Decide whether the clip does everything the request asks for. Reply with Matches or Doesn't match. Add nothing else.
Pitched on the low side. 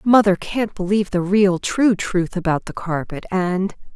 Doesn't match